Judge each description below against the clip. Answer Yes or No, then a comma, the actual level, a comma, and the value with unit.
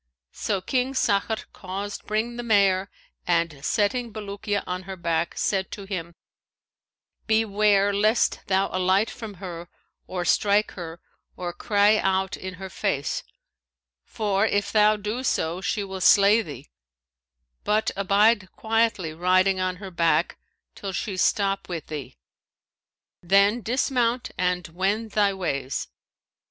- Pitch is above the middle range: Yes, high, 195 Hz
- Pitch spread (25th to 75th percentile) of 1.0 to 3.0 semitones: Yes, narrow, 2.6 semitones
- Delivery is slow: Yes, slow, 130 wpm